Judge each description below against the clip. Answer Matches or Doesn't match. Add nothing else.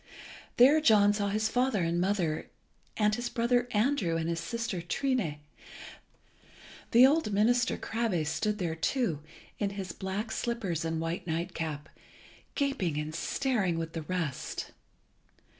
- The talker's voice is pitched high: Matches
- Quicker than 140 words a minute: Doesn't match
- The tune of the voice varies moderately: Doesn't match